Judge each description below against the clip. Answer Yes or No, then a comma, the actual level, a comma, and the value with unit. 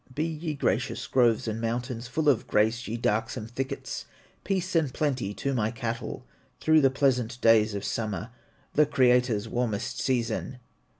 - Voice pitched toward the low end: Yes, low, 125 Hz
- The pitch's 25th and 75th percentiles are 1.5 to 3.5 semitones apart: Yes, average, 3.2 semitones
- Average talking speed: Yes, average, 155 wpm